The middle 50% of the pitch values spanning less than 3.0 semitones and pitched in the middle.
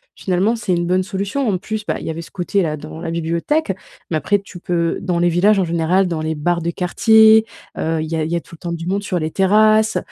No: average, 3.3 semitones; medium, 180 Hz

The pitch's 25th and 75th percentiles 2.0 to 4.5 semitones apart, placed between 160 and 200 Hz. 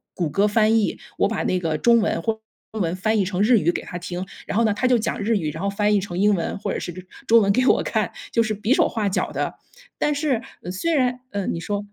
No: average, 3.4 semitones; high, 210 Hz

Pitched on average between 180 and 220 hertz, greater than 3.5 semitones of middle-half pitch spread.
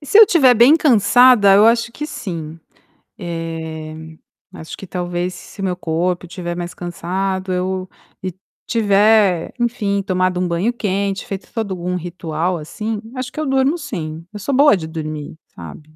Yes: medium, 185 Hz; average, 4.6 semitones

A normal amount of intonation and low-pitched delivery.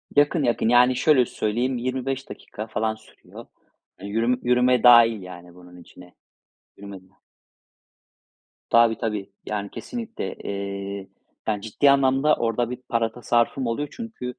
Yes: average, 4.0 semitones; low, 115 Hz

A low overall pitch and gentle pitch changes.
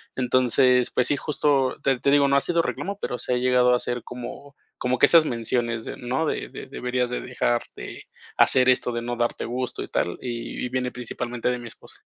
Yes: low, 125 Hz; narrow, 1.4 semitones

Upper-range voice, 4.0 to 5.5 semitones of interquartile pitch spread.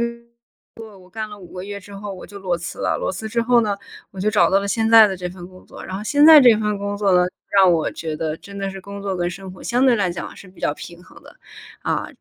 No: high, 200 Hz; average, 2.7 semitones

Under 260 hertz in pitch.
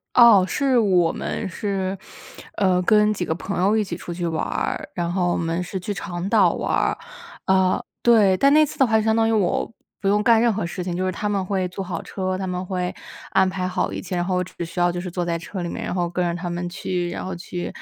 Yes: medium, 185 Hz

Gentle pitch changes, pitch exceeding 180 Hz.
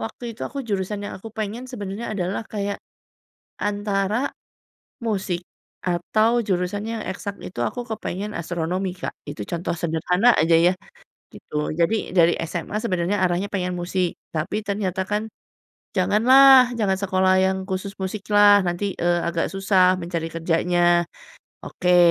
No: average, 3.0 semitones; high, 190 Hz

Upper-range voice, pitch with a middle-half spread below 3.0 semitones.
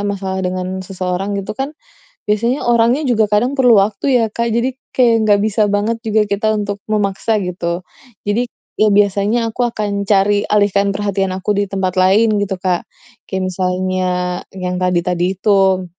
Yes: high, 200 Hz; narrow, 2.5 semitones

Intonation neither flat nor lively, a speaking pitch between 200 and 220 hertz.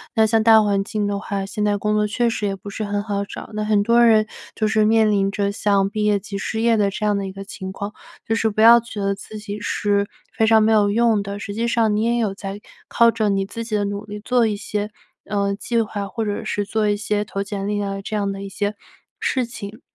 No: narrow, 1.6 semitones; high, 210 Hz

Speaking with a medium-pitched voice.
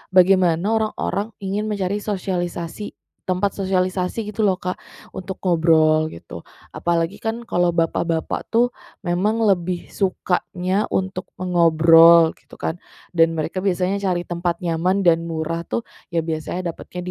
Yes: medium, 180 Hz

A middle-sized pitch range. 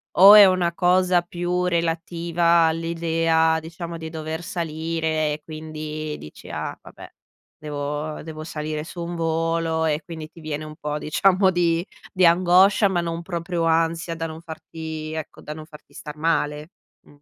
No: narrow, 1.6 semitones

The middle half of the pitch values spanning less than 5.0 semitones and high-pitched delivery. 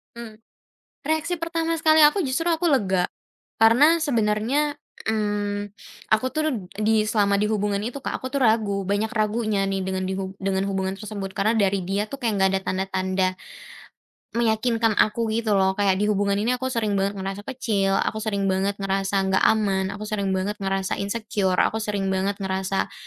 Yes: average, 3.0 semitones; high, 205 Hz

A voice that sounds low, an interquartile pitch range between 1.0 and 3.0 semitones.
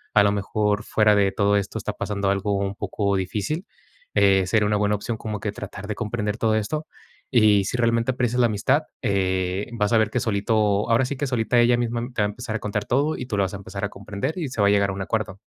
Yes: low, 105 Hz; narrow, 2.6 semitones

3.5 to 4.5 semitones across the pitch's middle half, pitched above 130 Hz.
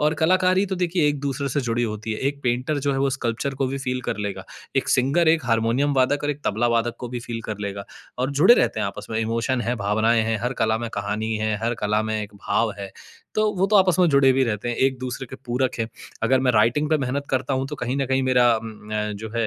No: average, 3.8 semitones; low, 125 Hz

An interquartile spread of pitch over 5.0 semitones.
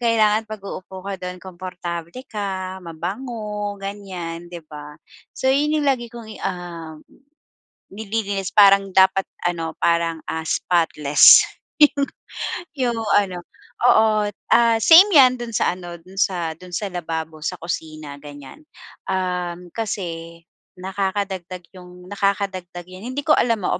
No: average, 3.7 semitones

